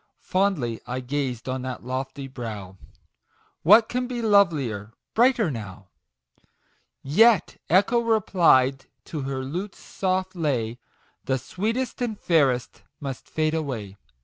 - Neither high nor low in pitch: Yes, medium, 145 Hz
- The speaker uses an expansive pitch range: Yes, wide, 8.0 semitones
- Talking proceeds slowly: Yes, slow, 130 wpm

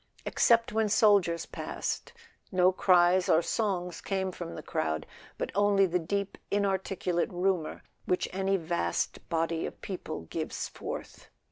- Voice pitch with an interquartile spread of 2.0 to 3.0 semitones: Yes, narrow, 2.6 semitones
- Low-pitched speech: No, medium, 185 Hz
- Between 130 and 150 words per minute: Yes, average, 140 wpm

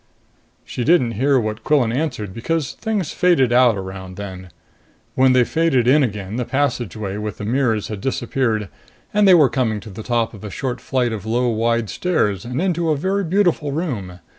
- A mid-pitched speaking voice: No, low, 120 Hz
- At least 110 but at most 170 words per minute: No, average, 190 wpm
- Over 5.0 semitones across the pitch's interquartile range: Yes, wide, 5.5 semitones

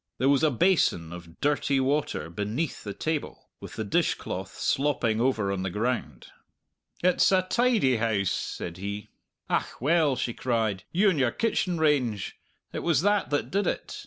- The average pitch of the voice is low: Yes, low, 130 Hz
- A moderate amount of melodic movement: No, wide, 7.5 semitones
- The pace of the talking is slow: No, average, 165 wpm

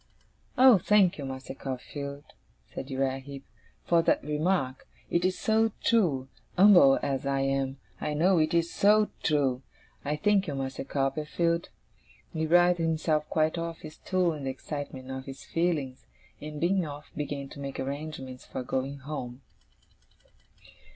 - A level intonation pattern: No, average, 4.0 semitones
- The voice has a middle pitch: Yes, medium, 150 Hz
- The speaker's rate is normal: Yes, average, 150 wpm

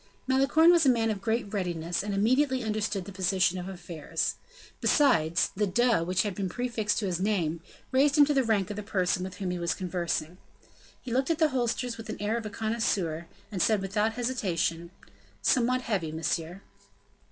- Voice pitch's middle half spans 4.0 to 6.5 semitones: Yes, average, 5.0 semitones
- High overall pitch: Yes, high, 205 Hz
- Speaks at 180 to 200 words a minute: Yes, average, 190 wpm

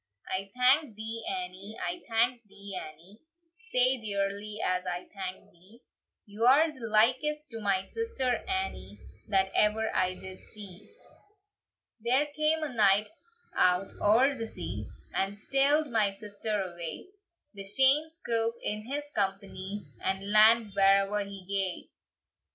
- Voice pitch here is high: Yes, high, 210 Hz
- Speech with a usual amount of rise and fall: Yes, average, 4.5 semitones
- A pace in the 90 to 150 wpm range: Yes, slow, 135 wpm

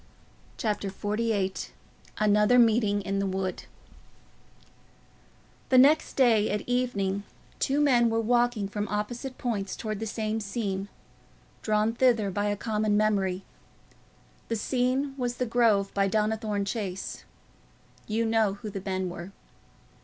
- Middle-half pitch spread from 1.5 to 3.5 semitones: Yes, average, 3.0 semitones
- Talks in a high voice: Yes, high, 215 Hz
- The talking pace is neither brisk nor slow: No, slow, 130 wpm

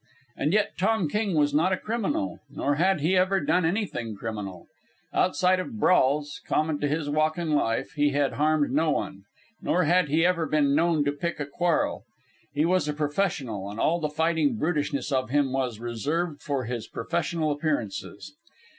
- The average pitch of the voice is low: No, medium, 150 Hz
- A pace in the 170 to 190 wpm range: Yes, average, 180 wpm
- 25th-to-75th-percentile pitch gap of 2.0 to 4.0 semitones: Yes, average, 3.5 semitones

